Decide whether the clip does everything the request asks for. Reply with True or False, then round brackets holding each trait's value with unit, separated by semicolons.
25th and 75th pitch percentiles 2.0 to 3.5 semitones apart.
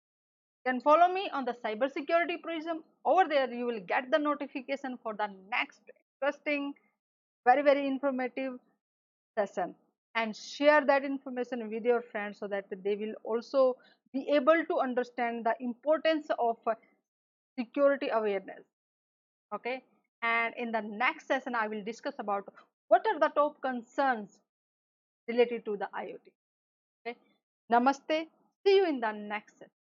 False (4.1 semitones)